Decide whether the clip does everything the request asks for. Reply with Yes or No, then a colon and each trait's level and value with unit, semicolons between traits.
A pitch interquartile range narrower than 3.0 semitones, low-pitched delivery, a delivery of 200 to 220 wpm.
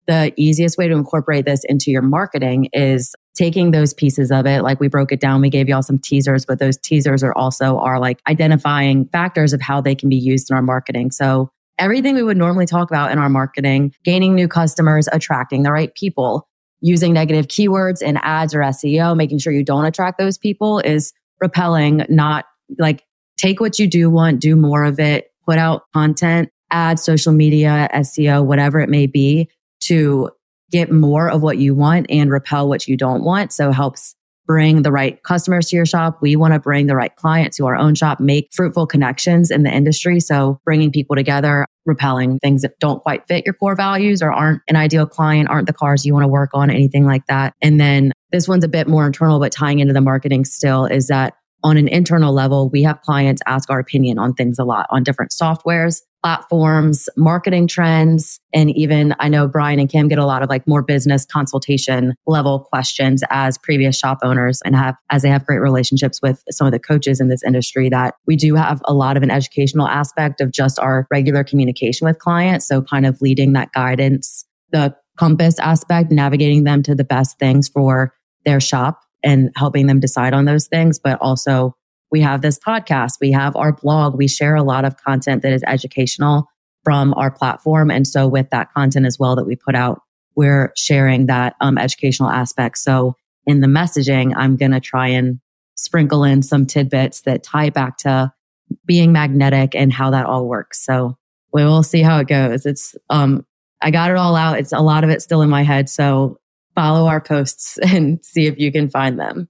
No: narrow, 2.6 semitones; medium, 145 Hz; fast, 205 wpm